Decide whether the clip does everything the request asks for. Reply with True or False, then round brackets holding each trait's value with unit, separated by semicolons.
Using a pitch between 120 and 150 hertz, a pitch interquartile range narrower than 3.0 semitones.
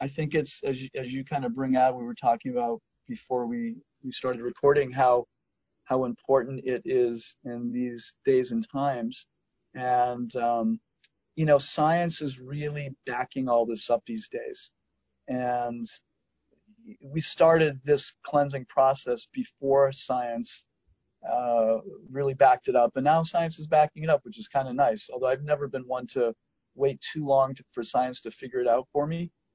False (135 Hz; 3.4 semitones)